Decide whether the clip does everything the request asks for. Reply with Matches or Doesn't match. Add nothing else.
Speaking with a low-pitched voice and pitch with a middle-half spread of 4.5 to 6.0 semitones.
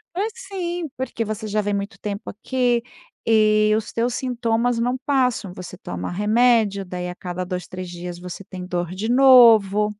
Doesn't match